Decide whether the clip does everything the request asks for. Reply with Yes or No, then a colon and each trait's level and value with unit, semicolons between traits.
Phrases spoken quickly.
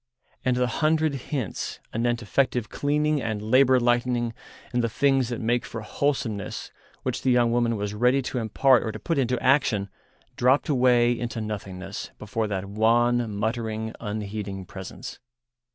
No: average, 150 wpm